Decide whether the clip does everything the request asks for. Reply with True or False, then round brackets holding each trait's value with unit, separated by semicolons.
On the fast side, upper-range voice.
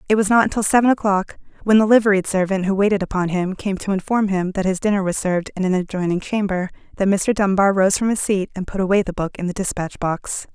True (245 wpm; 195 Hz)